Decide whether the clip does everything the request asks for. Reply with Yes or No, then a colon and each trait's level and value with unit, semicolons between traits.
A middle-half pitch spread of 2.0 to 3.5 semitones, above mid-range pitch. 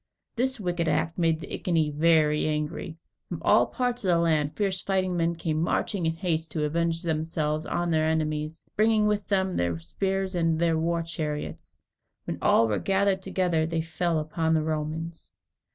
No: average, 2.7 semitones; medium, 165 Hz